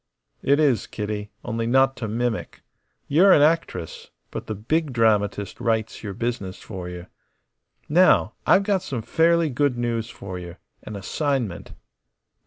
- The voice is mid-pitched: No, low, 115 Hz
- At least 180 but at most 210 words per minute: No, average, 145 wpm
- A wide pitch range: Yes, wide, 5.7 semitones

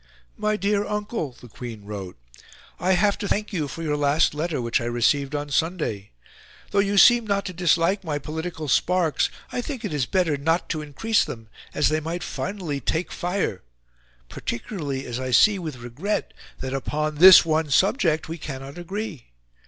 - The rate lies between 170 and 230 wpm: Yes, average, 175 wpm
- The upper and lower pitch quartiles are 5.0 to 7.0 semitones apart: Yes, wide, 5.4 semitones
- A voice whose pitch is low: No, medium, 160 Hz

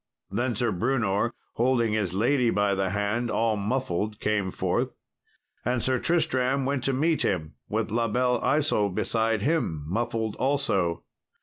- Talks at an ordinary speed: Yes, average, 145 wpm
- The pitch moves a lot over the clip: No, average, 4.1 semitones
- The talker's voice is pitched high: No, low, 115 Hz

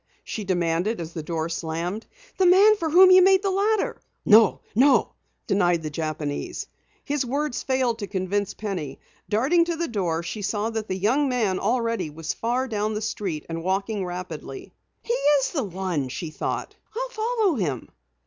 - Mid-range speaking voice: No, high, 210 Hz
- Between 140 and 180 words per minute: Yes, average, 170 wpm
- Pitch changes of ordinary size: No, wide, 8.4 semitones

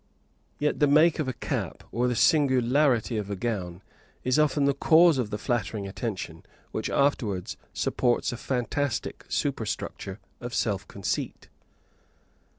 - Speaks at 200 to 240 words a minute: No, average, 140 wpm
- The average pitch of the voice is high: No, low, 125 Hz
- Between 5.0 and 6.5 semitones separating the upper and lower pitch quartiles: Yes, average, 5.3 semitones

